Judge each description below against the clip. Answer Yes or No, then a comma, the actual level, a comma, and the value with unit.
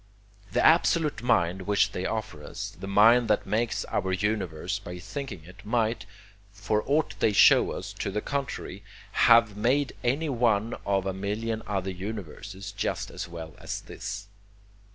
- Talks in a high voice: No, low, 105 Hz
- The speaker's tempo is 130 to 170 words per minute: Yes, average, 155 wpm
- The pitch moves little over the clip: No, average, 3.5 semitones